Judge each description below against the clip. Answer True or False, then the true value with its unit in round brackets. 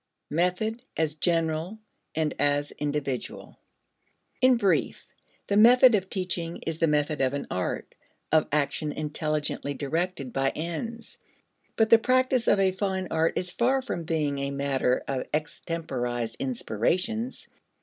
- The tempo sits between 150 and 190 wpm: False (135 wpm)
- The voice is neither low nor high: True (160 Hz)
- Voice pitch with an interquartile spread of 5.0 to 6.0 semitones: True (5.3 semitones)